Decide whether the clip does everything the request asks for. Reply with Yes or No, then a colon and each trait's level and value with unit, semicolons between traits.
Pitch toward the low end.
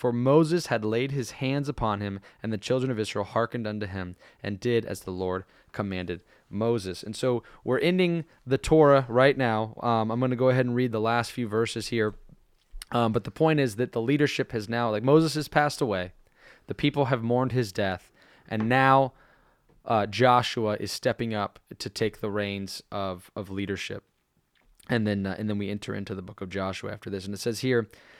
Yes: low, 115 Hz